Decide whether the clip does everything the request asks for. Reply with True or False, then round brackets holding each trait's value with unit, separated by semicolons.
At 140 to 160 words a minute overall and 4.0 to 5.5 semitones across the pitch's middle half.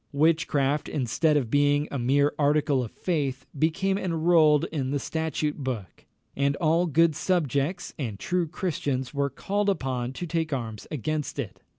False (155 wpm; 3.3 semitones)